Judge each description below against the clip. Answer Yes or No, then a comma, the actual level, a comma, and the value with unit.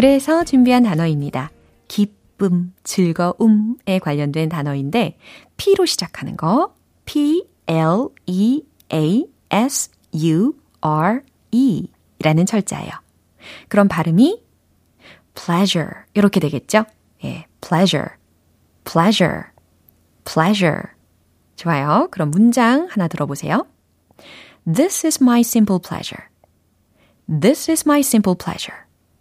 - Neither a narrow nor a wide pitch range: No, wide, 7.6 semitones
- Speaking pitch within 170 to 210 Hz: Yes, high, 190 Hz